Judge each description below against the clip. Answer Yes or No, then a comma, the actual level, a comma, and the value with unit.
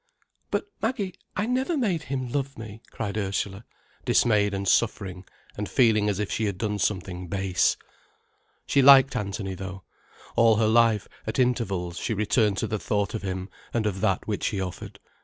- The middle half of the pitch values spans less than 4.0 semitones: Yes, average, 3.6 semitones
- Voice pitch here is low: Yes, low, 105 Hz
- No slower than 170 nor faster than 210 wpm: Yes, average, 175 wpm